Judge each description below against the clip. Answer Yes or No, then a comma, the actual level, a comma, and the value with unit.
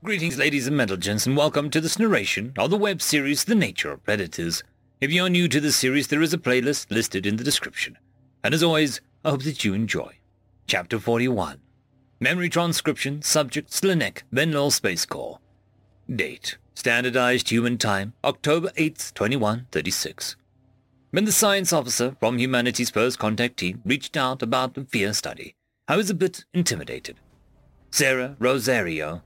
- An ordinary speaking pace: Yes, average, 165 wpm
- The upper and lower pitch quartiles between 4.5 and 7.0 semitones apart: Yes, average, 5.1 semitones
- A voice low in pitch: Yes, low, 130 Hz